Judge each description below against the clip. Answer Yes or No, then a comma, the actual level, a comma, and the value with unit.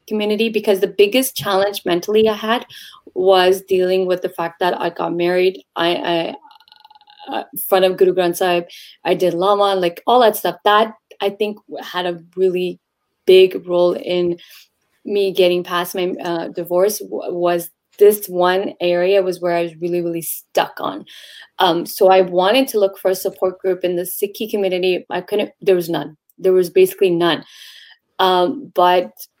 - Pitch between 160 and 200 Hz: Yes, medium, 185 Hz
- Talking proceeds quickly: Yes, fast, 175 wpm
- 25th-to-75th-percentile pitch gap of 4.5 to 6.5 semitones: No, narrow, 2.4 semitones